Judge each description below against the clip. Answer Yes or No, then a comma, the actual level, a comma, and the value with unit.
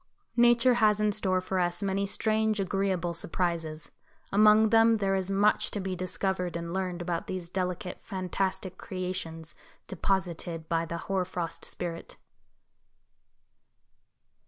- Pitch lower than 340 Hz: Yes, medium, 185 Hz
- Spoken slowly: Yes, slow, 130 wpm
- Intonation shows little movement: Yes, narrow, 2.3 semitones